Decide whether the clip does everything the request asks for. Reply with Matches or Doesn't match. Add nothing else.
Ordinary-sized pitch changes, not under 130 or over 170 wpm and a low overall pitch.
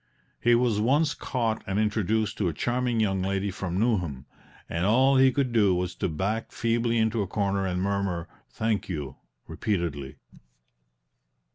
Matches